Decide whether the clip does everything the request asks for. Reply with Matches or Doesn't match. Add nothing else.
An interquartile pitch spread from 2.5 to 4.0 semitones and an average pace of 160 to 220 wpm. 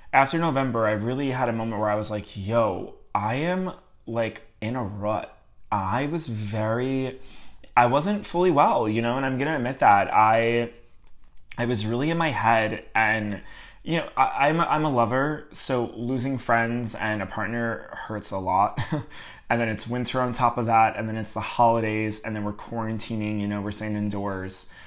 Matches